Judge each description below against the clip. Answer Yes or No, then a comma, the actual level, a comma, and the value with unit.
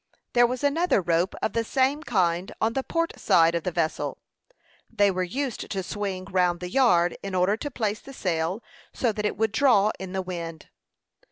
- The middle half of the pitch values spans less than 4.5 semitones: No, average, 5.2 semitones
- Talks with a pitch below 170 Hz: No, high, 200 Hz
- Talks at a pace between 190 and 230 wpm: Yes, average, 195 wpm